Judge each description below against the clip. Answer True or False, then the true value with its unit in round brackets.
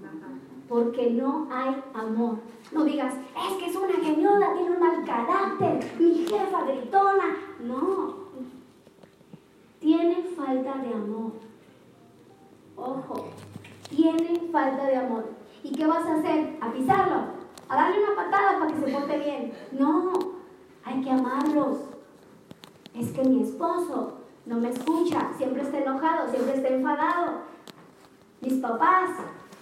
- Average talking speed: False (130 wpm)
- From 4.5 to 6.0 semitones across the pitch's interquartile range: True (5.1 semitones)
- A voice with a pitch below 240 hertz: False (300 Hz)